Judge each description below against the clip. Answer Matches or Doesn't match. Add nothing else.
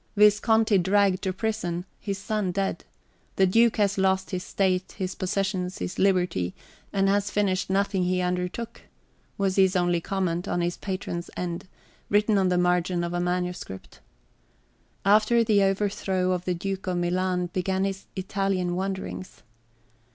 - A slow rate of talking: Doesn't match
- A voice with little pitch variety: Matches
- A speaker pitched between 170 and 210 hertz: Matches